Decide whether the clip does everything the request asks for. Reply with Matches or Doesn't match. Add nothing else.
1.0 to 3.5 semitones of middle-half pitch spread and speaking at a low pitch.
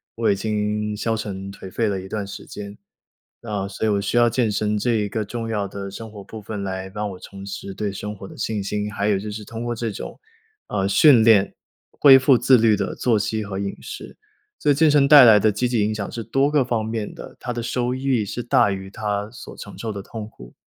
Matches